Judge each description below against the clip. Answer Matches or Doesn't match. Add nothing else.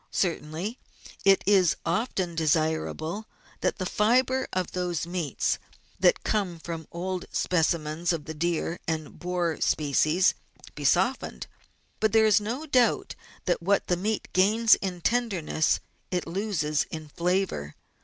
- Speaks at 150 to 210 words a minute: Doesn't match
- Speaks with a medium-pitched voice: Matches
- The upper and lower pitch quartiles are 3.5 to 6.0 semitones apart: Matches